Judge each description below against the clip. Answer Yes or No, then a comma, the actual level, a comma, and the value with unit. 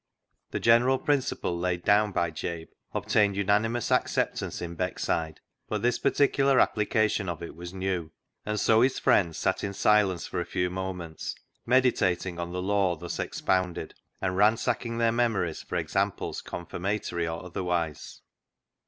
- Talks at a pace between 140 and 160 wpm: Yes, average, 150 wpm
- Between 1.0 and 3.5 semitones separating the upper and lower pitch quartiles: No, average, 4.0 semitones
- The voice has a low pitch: Yes, very low, 95 Hz